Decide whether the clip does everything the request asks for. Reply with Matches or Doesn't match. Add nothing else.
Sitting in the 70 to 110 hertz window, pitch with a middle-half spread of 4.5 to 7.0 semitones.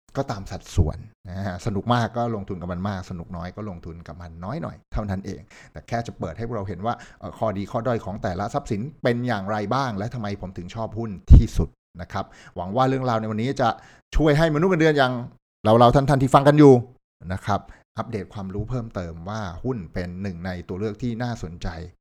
Matches